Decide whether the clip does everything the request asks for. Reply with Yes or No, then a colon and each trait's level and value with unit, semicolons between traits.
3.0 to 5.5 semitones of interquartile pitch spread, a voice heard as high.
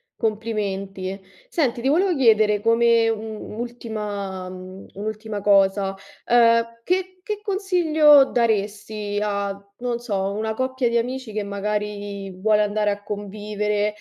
No: narrow, 2.6 semitones; high, 215 Hz